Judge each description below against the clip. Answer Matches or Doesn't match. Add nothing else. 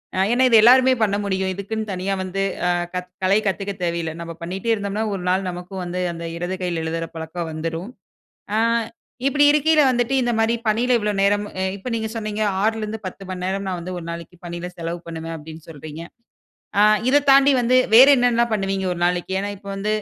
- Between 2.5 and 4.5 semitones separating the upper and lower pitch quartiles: Matches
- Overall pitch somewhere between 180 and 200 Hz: Matches